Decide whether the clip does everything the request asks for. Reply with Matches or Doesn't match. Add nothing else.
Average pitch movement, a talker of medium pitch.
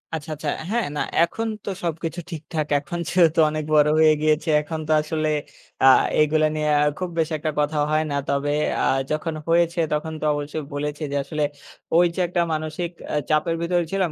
Doesn't match